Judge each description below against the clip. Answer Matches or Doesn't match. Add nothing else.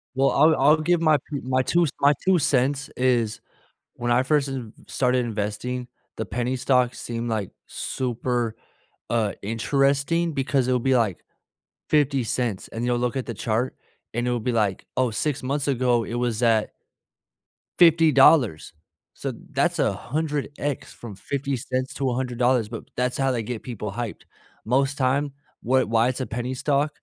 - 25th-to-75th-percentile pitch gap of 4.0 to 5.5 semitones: Doesn't match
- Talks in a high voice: Doesn't match